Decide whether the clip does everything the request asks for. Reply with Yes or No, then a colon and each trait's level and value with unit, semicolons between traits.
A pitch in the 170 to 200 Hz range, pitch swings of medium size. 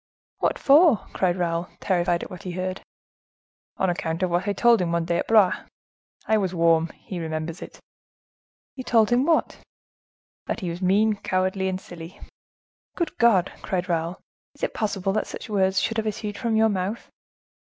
Yes: high, 190 Hz; average, 3.6 semitones